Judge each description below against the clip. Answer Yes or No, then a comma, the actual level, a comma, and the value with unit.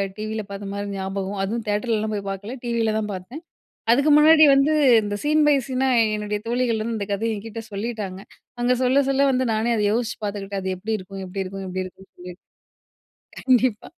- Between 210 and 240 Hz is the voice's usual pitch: Yes, high, 215 Hz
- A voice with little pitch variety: No, average, 3.6 semitones